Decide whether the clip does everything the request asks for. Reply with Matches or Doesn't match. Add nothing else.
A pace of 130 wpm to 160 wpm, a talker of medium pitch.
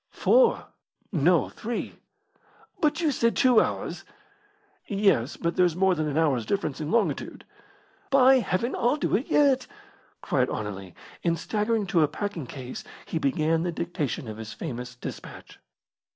Matches